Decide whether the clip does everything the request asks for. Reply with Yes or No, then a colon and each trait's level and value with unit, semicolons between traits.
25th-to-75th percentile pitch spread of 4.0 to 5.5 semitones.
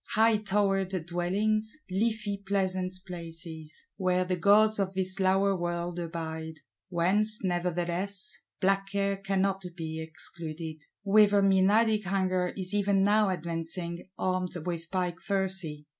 No: narrow, 2.5 semitones